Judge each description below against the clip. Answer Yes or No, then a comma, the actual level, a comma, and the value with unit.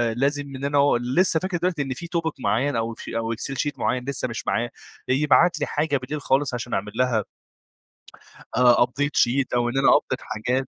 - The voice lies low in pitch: Yes, low, 130 Hz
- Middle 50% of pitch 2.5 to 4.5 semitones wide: Yes, average, 3.1 semitones